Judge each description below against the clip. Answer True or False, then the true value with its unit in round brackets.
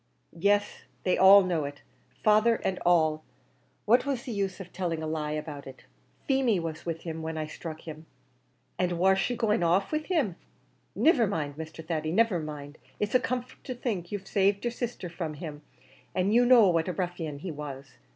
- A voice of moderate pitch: True (180 Hz)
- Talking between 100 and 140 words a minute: False (190 wpm)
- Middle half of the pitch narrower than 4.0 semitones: False (5.0 semitones)